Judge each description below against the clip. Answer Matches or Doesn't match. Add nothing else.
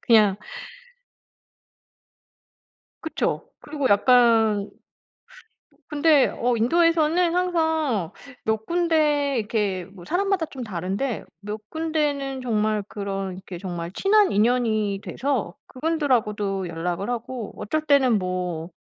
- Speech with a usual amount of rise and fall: Doesn't match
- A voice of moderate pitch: Doesn't match